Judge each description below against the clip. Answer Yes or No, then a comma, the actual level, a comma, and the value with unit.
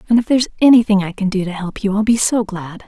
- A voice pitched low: No, high, 210 Hz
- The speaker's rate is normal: No, fast, 290 wpm